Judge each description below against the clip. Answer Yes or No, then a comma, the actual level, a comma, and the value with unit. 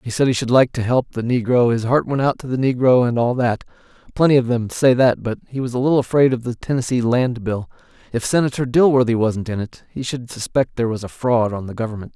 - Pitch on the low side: Yes, low, 120 Hz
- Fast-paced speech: Yes, fast, 245 wpm